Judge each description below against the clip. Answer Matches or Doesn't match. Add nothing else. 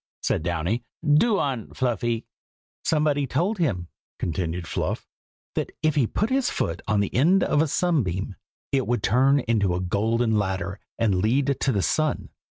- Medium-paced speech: Matches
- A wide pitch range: Matches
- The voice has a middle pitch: Doesn't match